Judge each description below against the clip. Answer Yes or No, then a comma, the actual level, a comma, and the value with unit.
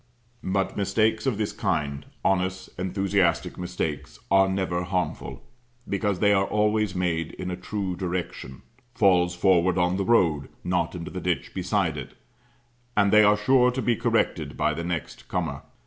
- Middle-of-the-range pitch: No, very low, 95 Hz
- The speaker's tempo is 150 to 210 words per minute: Yes, average, 160 wpm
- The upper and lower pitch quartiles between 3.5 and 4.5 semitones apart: No, narrow, 2.6 semitones